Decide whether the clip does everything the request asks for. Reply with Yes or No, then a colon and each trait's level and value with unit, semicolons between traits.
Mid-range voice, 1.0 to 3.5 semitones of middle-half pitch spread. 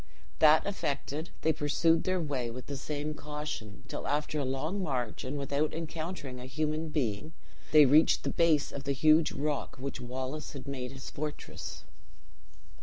Yes: medium, 145 Hz; average, 2.7 semitones